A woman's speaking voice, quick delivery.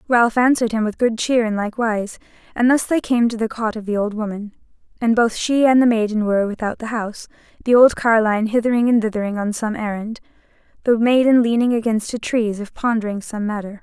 Yes: female; fast, 215 wpm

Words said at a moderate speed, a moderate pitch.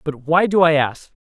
No: fast, 245 wpm; medium, 155 Hz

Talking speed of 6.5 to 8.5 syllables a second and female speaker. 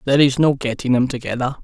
No: 6.8 syllables/s; male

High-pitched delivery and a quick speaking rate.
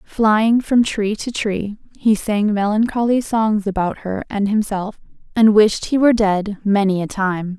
No: high, 210 Hz; average, 165 wpm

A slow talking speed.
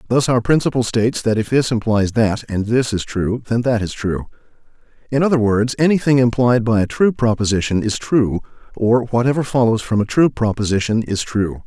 No: average, 190 wpm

